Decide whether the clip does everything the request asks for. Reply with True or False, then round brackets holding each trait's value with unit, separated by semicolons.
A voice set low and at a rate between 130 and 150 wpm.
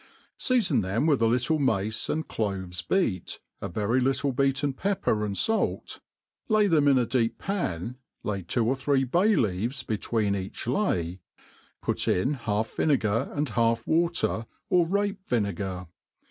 True (120 Hz; 145 wpm)